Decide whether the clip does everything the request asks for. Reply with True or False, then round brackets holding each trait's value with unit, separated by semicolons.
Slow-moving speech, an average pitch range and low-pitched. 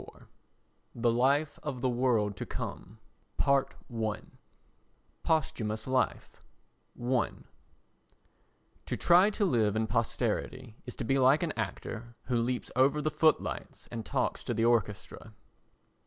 True (125 wpm; 3.1 semitones; 125 Hz)